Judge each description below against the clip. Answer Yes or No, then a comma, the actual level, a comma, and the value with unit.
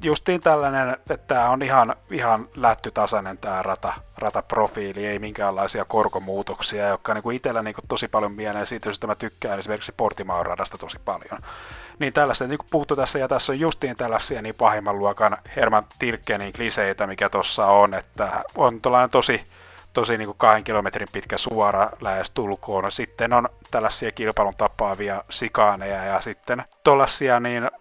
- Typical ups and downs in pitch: Yes, average, 3.8 semitones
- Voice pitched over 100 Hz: Yes, low, 110 Hz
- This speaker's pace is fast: Yes, fast, 160 wpm